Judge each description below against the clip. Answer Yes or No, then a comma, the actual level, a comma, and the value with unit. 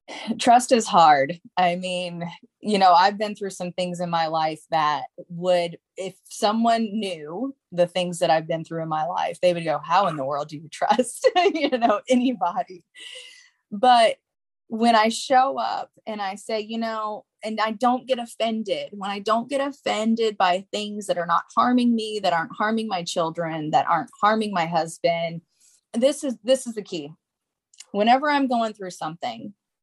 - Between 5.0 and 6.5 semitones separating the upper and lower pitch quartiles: Yes, wide, 5.6 semitones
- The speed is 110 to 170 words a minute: No, average, 180 wpm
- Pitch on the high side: Yes, high, 210 Hz